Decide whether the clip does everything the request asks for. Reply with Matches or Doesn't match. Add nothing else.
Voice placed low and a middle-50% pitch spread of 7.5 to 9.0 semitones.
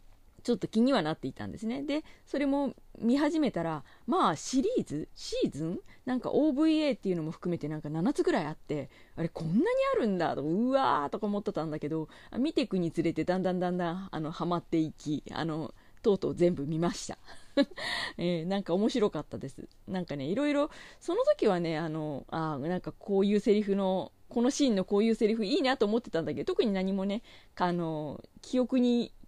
Doesn't match